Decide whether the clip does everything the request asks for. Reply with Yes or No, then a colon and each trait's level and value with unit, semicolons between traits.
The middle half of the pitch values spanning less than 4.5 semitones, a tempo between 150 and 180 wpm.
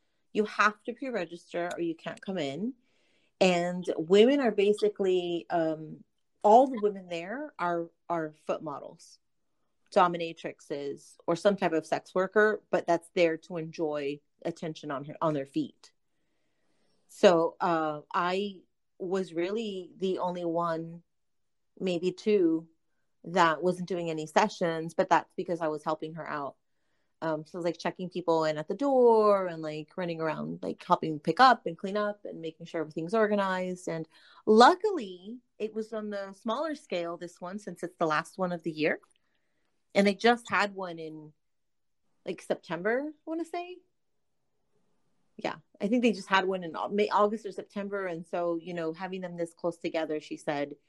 Yes: average, 3.9 semitones; average, 170 wpm